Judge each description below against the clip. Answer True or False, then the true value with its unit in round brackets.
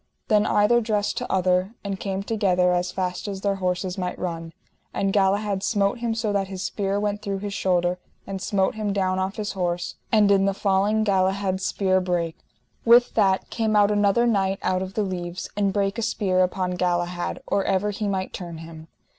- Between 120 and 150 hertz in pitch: False (195 Hz)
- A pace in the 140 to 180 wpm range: False (195 wpm)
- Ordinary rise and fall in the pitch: False (2.0 semitones)